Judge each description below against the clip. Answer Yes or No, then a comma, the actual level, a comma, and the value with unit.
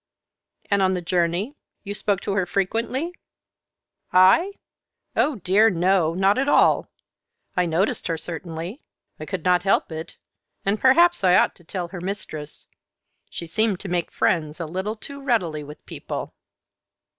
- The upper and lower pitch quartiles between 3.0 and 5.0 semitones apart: Yes, average, 3.9 semitones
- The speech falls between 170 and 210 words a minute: No, average, 155 wpm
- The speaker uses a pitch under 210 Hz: Yes, high, 190 Hz